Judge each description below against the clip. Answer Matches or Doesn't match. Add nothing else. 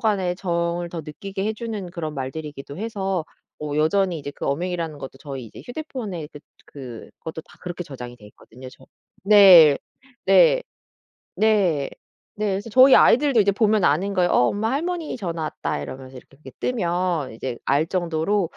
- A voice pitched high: Doesn't match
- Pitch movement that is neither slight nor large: Doesn't match